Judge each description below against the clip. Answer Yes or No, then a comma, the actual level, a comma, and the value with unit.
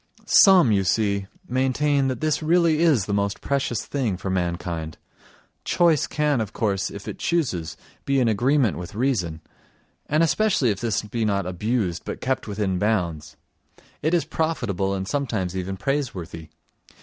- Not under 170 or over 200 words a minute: No, average, 155 wpm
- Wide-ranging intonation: Yes, wide, 6.9 semitones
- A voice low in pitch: Yes, low, 110 Hz